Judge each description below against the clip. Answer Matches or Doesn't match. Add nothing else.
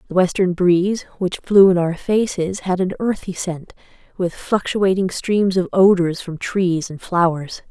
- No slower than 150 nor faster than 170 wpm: Matches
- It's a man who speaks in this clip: Doesn't match